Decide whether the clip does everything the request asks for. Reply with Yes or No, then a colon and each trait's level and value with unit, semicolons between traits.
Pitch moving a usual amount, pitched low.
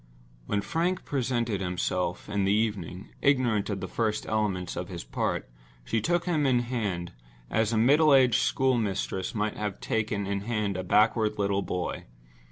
Yes: average, 3.7 semitones; low, 110 Hz